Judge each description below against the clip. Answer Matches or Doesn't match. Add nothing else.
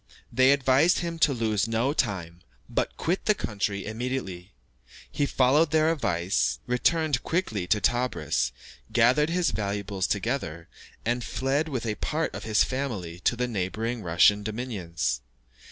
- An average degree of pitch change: Doesn't match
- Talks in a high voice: Doesn't match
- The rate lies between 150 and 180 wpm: Doesn't match